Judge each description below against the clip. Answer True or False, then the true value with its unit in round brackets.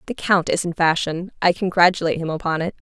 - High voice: False (170 Hz)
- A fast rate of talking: True (210 wpm)